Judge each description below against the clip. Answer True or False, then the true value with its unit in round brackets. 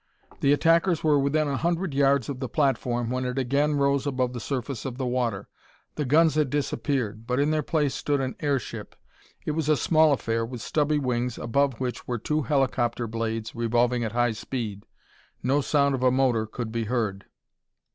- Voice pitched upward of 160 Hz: False (130 Hz)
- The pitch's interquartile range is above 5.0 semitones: False (3.3 semitones)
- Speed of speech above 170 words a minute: True (190 wpm)